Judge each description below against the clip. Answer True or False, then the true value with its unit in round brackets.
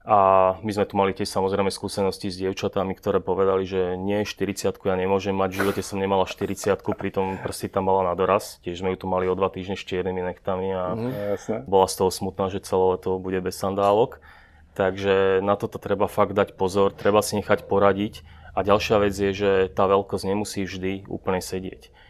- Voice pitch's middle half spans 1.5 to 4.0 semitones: False (1.0 semitones)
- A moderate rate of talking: False (200 wpm)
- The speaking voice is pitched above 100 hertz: False (95 Hz)